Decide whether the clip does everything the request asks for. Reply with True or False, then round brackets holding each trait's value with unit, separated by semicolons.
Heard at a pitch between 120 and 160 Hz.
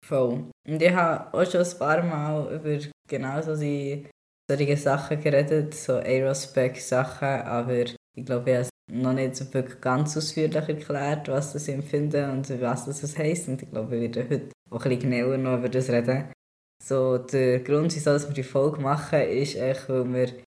True (135 Hz)